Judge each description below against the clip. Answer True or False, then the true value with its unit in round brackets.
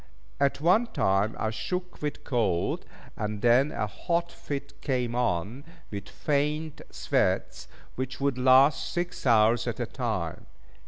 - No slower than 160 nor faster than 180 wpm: False (140 wpm)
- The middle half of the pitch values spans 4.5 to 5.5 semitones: True (5.2 semitones)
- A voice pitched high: False (130 Hz)